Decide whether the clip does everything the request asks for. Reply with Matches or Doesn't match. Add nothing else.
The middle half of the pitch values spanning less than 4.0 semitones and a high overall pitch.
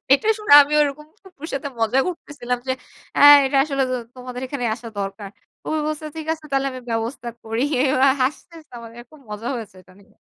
Doesn't match